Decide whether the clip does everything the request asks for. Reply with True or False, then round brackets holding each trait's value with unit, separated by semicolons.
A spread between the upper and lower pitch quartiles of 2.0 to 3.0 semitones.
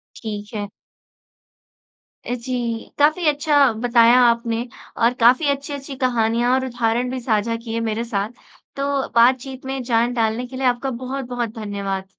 True (2.4 semitones)